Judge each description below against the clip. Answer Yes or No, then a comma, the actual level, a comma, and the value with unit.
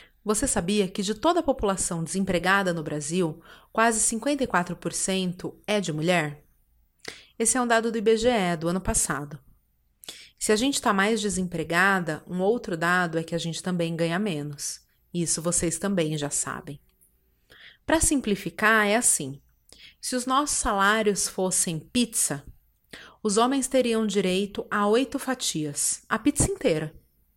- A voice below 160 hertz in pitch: No, high, 190 Hz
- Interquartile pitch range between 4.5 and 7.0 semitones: Yes, wide, 5.4 semitones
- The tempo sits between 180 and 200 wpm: No, average, 145 wpm